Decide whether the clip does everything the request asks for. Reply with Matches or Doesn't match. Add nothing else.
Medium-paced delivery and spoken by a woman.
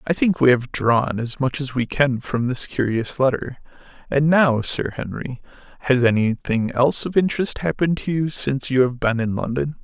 Doesn't match